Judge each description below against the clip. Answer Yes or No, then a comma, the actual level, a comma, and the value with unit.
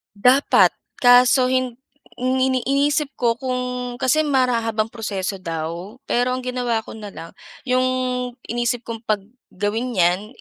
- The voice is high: Yes, high, 245 Hz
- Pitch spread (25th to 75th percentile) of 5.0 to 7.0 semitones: No, average, 2.9 semitones